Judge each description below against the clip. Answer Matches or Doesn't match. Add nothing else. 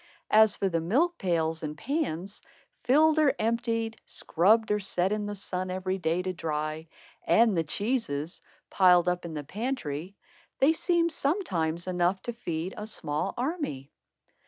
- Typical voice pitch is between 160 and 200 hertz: Matches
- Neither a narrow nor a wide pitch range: Doesn't match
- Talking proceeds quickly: Doesn't match